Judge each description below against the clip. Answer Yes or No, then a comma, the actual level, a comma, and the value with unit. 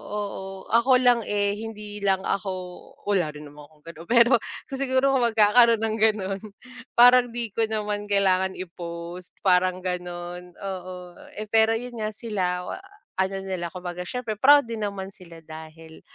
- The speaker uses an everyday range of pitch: Yes, average, 3.9 semitones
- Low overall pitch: No, high, 200 Hz